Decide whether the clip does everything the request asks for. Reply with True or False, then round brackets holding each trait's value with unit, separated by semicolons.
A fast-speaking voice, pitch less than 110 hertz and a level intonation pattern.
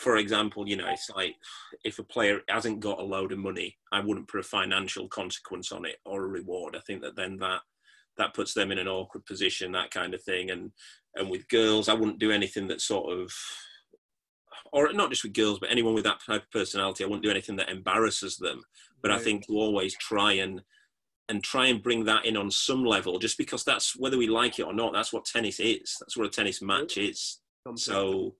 True (230 wpm; 100 Hz; 2.3 semitones)